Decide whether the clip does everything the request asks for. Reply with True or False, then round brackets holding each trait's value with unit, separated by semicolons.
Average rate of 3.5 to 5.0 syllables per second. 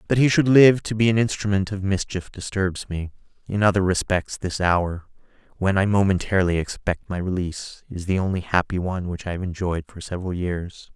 False (5.5 syllables/s)